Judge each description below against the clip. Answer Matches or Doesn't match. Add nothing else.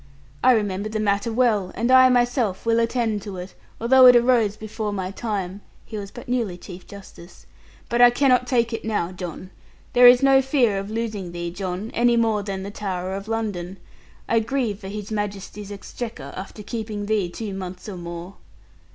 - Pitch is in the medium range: Doesn't match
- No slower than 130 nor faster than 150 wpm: Doesn't match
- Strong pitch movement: Doesn't match